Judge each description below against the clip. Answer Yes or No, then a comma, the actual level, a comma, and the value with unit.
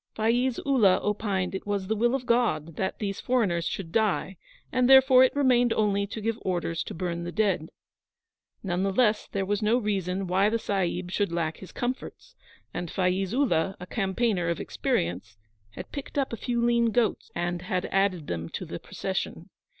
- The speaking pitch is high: Yes, high, 200 Hz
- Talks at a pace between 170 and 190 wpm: Yes, average, 185 wpm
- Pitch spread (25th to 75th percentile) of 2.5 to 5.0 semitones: Yes, average, 4.6 semitones